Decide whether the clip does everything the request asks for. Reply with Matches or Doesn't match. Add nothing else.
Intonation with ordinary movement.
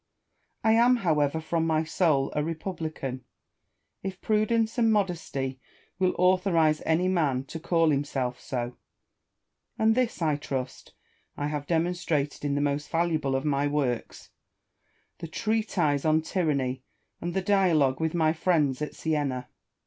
Matches